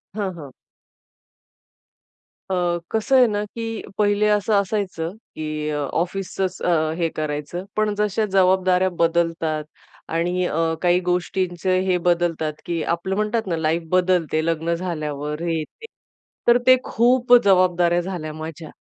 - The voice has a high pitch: No, medium, 175 Hz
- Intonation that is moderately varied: Yes, average, 3.3 semitones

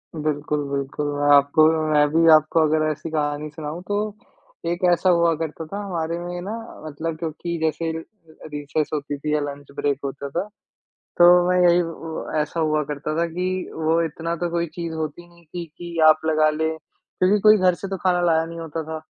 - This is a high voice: No, medium, 160 Hz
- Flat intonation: Yes, narrow, 2.2 semitones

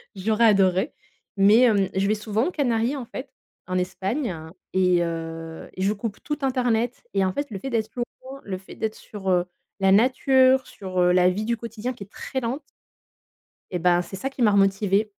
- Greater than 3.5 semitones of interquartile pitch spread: Yes, average, 4.5 semitones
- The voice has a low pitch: No, high, 210 Hz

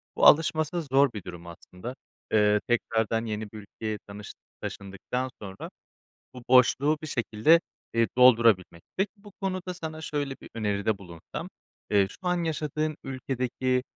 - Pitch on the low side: Yes, low, 125 Hz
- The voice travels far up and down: Yes, wide, 6.5 semitones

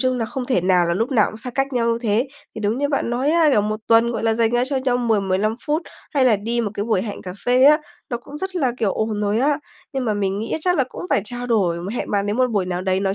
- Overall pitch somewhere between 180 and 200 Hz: No, high, 230 Hz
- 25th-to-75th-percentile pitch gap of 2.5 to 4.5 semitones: Yes, average, 4.0 semitones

